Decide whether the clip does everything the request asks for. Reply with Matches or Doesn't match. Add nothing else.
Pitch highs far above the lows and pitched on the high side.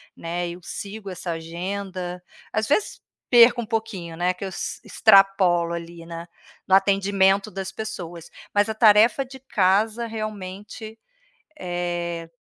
Doesn't match